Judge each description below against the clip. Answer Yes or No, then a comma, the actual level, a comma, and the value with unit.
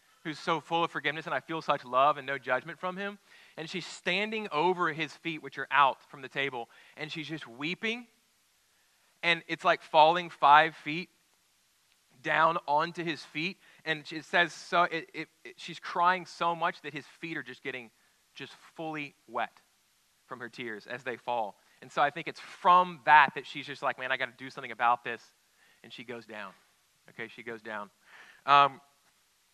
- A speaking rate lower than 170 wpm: No, average, 195 wpm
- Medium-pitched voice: Yes, medium, 155 Hz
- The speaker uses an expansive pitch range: No, average, 3.6 semitones